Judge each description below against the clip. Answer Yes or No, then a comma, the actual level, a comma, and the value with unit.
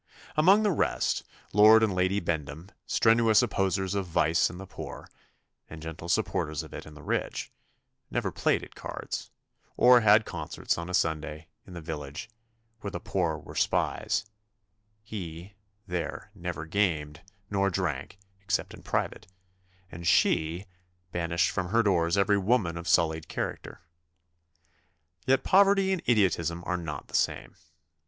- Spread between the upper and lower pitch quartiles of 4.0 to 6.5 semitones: Yes, average, 4.3 semitones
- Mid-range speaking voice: No, very low, 90 Hz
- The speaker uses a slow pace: No, average, 145 wpm